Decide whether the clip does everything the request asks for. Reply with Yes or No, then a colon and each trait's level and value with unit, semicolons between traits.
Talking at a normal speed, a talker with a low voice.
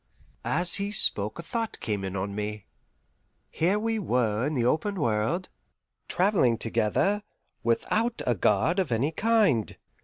No: average, 145 wpm; medium, 145 Hz